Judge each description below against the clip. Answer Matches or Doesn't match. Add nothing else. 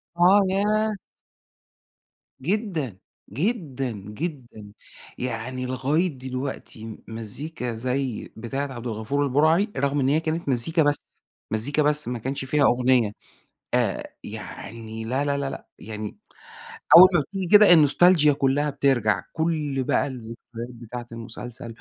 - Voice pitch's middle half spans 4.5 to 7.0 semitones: Matches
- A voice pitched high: Doesn't match